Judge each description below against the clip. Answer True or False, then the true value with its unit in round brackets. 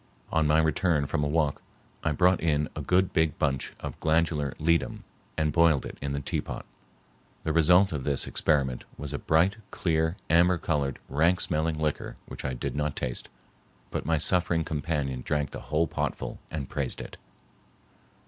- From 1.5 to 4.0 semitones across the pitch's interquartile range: True (2.4 semitones)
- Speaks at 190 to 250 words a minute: False (170 wpm)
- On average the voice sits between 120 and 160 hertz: False (80 Hz)